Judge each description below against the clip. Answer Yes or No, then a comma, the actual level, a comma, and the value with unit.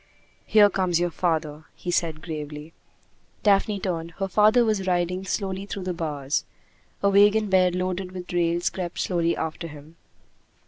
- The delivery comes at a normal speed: Yes, average, 150 wpm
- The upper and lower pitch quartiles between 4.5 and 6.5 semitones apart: No, average, 2.8 semitones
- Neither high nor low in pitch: Yes, medium, 180 Hz